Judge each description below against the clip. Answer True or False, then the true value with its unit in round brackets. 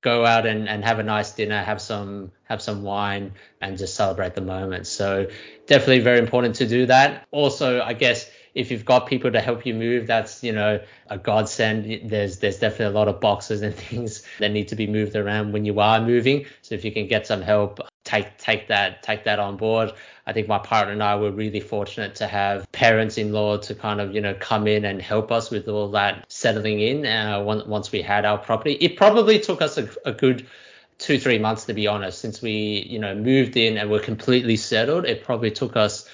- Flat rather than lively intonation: True (2.0 semitones)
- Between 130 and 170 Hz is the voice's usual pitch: False (110 Hz)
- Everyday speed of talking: False (225 wpm)